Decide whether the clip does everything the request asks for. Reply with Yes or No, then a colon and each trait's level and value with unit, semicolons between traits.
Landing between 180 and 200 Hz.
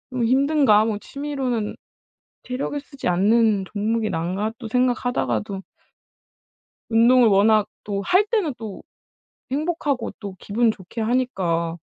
No: high, 225 Hz